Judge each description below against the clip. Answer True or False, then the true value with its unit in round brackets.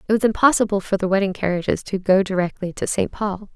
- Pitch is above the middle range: True (195 Hz)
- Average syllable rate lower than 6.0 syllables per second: False (6.3 syllables/s)